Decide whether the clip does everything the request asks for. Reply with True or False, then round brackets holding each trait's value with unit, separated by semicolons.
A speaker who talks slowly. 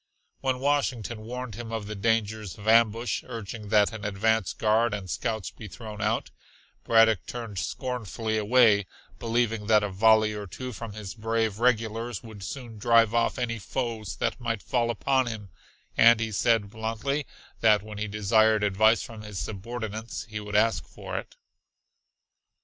False (160 wpm)